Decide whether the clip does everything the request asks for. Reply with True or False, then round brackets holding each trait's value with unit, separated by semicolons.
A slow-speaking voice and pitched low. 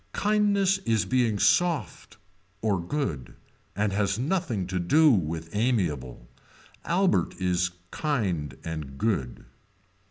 True (105 wpm; 100 Hz)